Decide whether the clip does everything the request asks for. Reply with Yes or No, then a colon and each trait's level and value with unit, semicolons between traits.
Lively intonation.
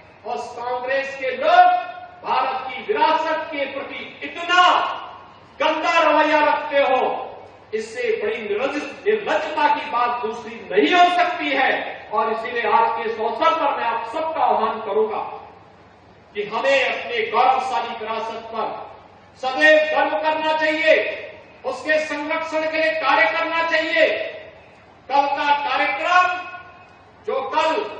Yes: wide, 5.7 semitones